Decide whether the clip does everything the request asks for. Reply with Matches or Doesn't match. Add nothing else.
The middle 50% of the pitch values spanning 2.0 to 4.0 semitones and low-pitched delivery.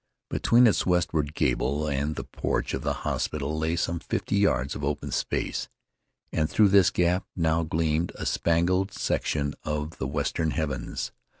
Matches